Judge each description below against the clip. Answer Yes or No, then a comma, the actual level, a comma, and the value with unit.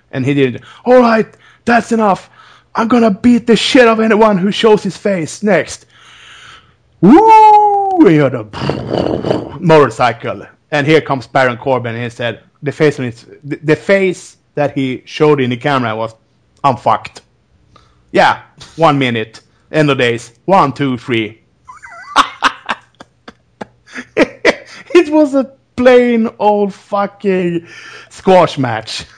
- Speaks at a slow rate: Yes, slow, 130 wpm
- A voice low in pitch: No, medium, 155 Hz